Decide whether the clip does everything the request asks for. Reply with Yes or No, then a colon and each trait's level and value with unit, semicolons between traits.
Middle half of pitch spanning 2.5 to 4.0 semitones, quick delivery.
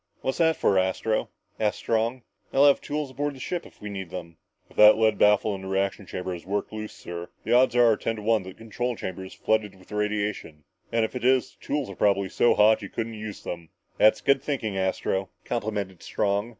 Yes: average, 3.4 semitones; fast, 225 wpm